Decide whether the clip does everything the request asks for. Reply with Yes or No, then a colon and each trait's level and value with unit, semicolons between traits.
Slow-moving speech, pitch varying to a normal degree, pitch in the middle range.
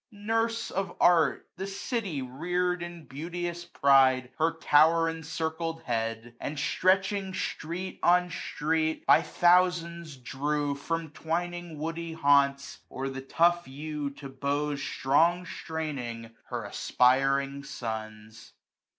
Yes: slow, 115 wpm; average, 3.9 semitones; medium, 160 Hz